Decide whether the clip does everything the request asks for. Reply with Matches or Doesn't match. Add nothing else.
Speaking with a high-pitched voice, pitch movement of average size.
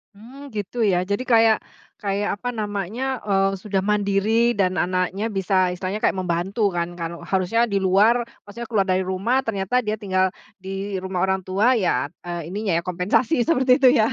Matches